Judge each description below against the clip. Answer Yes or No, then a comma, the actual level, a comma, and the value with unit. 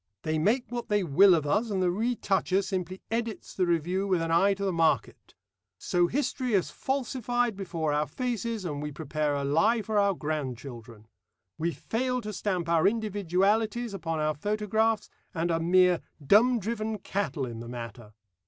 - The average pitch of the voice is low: No, high, 190 Hz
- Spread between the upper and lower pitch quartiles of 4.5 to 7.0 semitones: Yes, wide, 5.5 semitones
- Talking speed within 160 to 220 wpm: Yes, average, 170 wpm